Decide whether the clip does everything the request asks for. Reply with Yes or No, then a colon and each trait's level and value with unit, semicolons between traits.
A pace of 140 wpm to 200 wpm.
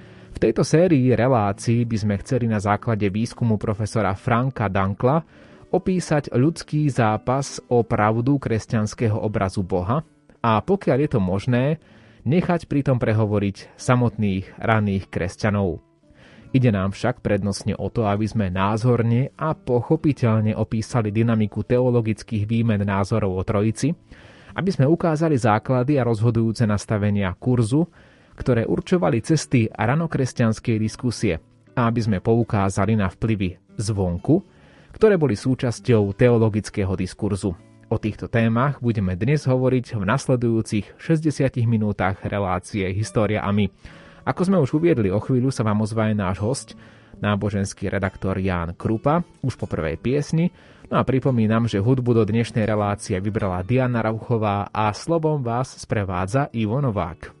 No: average, 130 wpm